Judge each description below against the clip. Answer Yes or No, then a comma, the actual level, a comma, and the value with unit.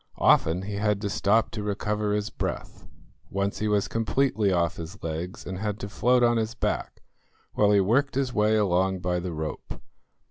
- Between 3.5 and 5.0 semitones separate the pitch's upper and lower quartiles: No, average, 2.7 semitones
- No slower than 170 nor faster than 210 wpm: Yes, average, 185 wpm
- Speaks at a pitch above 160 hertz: No, low, 105 Hz